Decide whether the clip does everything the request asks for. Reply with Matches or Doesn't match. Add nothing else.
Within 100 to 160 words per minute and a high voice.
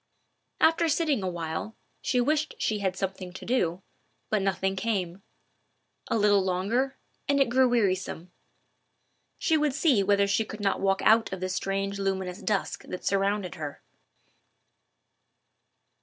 Matches